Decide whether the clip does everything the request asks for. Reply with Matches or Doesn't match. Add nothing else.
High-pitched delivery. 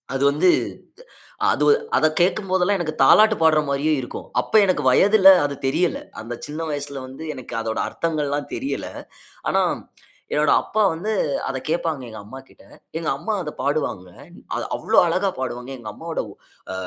Doesn't match